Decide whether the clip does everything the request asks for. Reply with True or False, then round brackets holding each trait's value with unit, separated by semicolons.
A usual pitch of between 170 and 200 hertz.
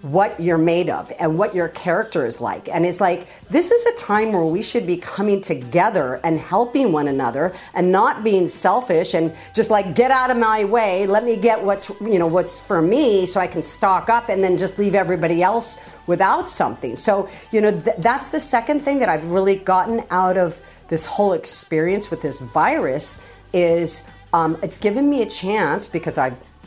True (190 Hz)